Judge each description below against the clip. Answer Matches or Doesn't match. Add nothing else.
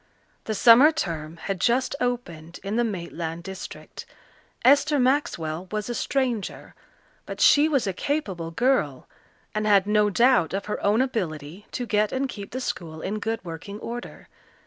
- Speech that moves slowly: Doesn't match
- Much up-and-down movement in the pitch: Matches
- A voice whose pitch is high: Matches